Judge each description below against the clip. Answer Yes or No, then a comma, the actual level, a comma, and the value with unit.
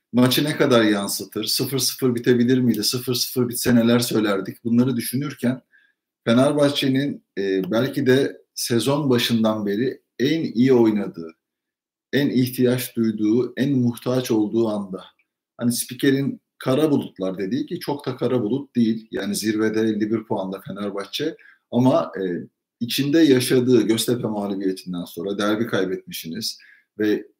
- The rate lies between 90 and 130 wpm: Yes, average, 125 wpm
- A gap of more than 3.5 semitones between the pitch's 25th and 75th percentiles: No, average, 3.2 semitones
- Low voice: Yes, low, 120 Hz